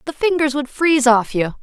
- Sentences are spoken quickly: Yes, fast, 220 wpm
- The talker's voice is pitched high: Yes, very high, 275 Hz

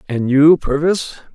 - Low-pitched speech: No, medium, 150 Hz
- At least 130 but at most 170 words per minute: Yes, slow, 135 wpm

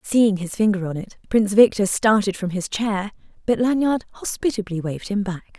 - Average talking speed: Yes, average, 185 wpm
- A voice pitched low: No, high, 205 Hz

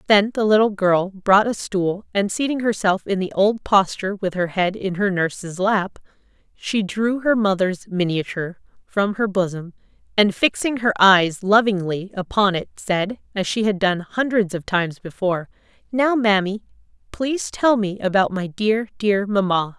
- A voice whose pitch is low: No, high, 200 Hz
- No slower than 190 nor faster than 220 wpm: No, average, 165 wpm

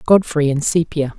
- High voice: No, medium, 155 Hz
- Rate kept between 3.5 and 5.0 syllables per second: Yes, 4.8 syllables/s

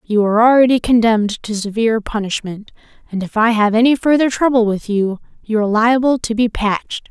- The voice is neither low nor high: No, high, 225 Hz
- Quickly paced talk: No, average, 185 wpm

